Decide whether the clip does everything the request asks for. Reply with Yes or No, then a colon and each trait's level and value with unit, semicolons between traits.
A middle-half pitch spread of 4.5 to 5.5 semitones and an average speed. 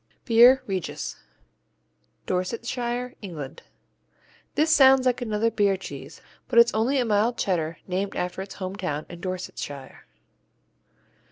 No: average, 4.9 semitones; slow, 115 wpm